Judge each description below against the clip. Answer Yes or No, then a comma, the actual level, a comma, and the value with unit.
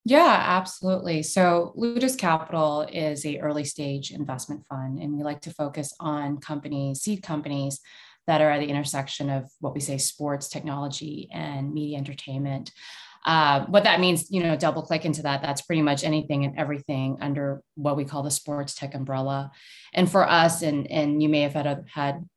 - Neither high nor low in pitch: Yes, medium, 150 Hz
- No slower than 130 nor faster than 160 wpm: No, average, 180 wpm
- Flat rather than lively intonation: Yes, narrow, 2.2 semitones